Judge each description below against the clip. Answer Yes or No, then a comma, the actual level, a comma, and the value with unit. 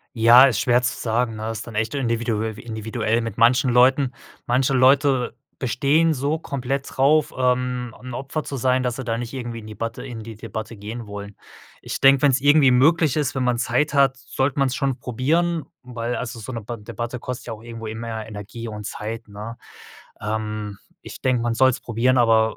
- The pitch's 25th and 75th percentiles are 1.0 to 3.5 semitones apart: Yes, average, 2.7 semitones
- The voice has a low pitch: Yes, low, 120 Hz